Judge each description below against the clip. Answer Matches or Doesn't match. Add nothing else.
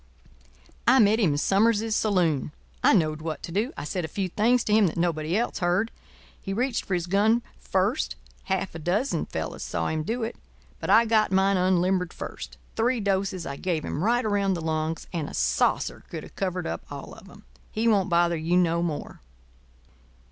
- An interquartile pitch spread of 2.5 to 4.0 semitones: Doesn't match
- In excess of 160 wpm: Matches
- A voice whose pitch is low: Doesn't match